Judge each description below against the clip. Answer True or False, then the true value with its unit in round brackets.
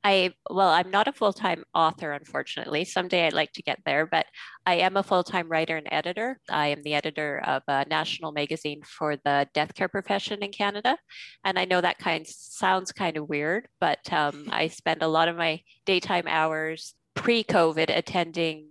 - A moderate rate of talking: True (190 wpm)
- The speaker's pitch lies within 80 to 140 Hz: False (165 Hz)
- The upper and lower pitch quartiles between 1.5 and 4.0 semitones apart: True (3.6 semitones)